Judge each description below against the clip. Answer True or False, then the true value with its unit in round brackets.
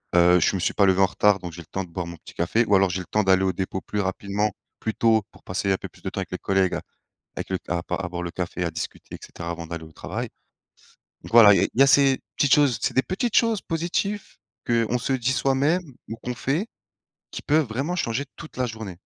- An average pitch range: False (6.6 semitones)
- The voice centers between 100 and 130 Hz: True (105 Hz)